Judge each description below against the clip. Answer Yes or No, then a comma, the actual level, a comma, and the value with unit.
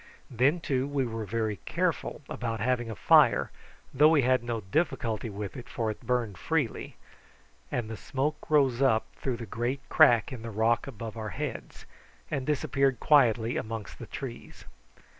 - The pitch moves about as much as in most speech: Yes, average, 3.3 semitones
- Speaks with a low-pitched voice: Yes, low, 120 Hz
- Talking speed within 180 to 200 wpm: No, average, 165 wpm